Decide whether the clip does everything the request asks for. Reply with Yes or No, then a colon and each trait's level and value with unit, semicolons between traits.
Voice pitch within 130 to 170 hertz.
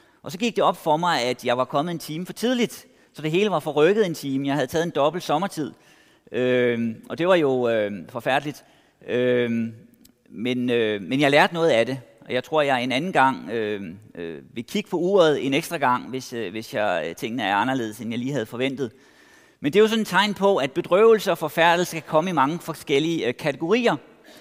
Yes: medium, 140 Hz